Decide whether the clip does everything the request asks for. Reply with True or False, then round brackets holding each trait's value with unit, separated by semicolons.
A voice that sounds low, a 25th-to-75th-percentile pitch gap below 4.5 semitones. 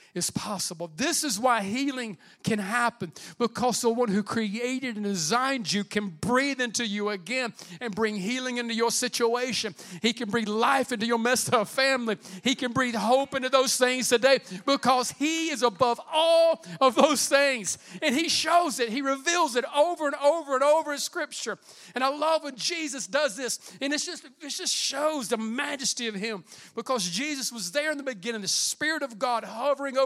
False (250 Hz; 4.0 semitones)